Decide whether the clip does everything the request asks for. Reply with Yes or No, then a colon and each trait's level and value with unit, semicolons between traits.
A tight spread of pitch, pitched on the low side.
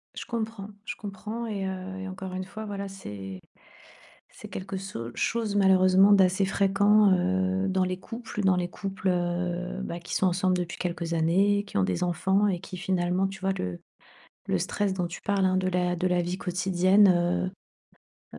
No: narrow, 1.7 semitones; medium, 185 Hz